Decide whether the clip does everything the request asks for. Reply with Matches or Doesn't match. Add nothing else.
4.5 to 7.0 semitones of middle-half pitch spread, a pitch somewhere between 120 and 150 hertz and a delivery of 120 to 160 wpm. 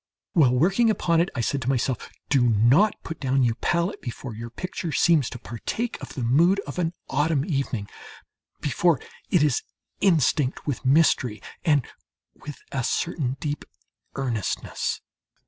Matches